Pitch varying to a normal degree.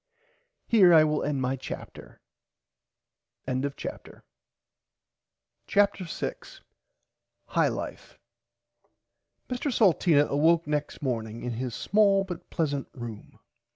No: wide, 6.4 semitones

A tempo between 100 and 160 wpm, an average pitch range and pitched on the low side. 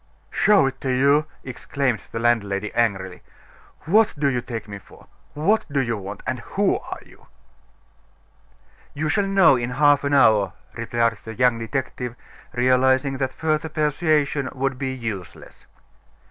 Yes: average, 145 wpm; average, 4.0 semitones; low, 130 Hz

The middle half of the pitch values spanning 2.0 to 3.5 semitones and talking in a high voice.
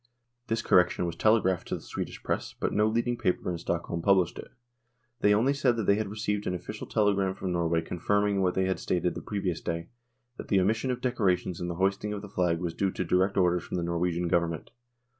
No: average, 2.9 semitones; very low, 95 Hz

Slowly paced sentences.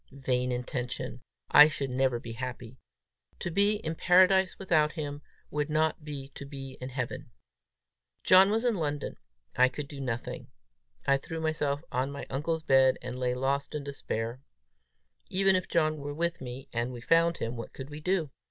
No: average, 175 wpm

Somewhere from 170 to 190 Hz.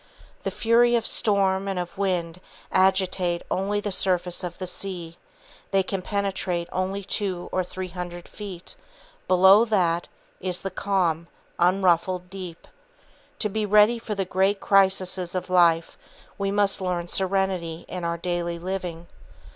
Yes: medium, 185 Hz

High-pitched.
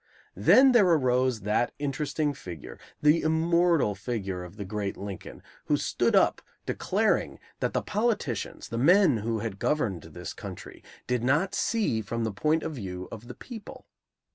No: low, 125 Hz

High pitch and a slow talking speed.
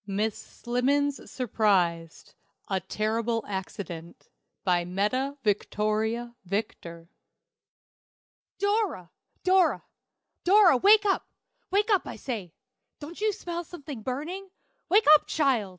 Yes: high, 240 Hz; slow, 105 wpm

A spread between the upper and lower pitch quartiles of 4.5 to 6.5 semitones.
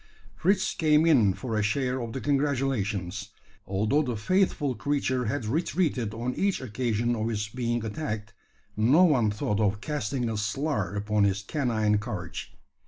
Yes: average, 5.1 semitones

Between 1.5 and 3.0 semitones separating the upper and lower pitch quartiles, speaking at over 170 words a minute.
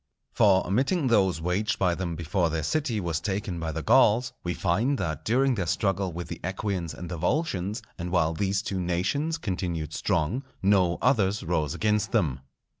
No: average, 3.8 semitones; average, 180 wpm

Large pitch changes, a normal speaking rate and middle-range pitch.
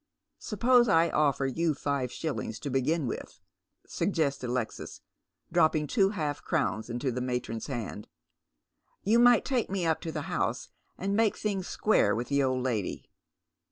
Yes: wide, 7.3 semitones; average, 160 wpm; medium, 150 Hz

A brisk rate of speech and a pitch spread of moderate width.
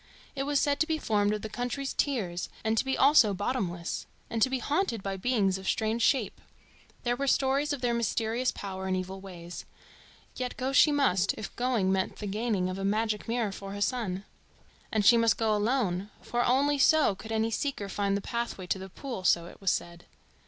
Yes: fast, 210 wpm; average, 4.8 semitones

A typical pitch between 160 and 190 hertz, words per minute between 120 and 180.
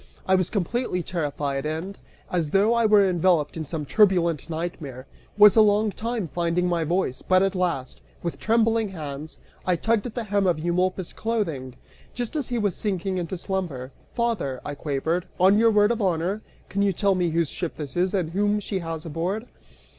No: medium, 185 Hz; average, 190 wpm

